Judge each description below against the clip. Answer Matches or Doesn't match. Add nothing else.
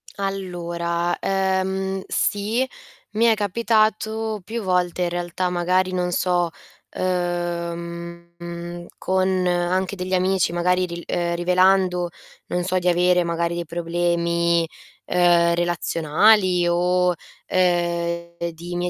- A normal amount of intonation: Doesn't match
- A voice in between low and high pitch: Matches